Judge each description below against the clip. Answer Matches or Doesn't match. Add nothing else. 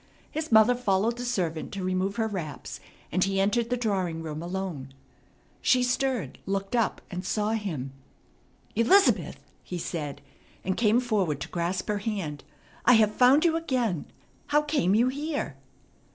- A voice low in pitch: Doesn't match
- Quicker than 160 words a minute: Doesn't match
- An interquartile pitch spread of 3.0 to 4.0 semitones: Doesn't match